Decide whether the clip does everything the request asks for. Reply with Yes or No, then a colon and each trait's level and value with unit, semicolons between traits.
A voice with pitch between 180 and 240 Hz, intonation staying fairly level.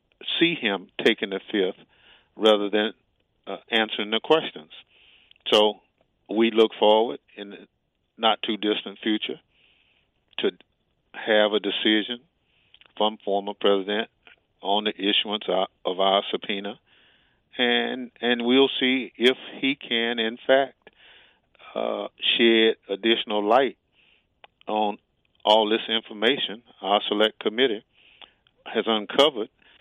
No: low, 110 Hz; narrow, 2.0 semitones